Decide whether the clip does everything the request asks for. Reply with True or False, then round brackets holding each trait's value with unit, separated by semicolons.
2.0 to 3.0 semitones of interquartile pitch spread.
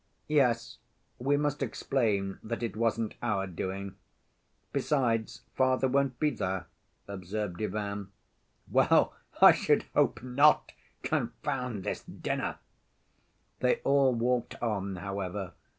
False (4.6 semitones)